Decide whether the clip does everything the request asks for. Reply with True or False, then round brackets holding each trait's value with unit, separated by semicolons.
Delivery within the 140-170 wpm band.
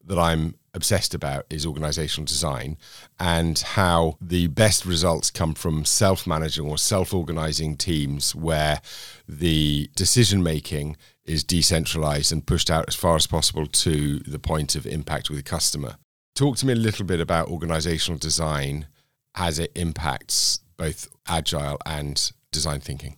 True (150 wpm)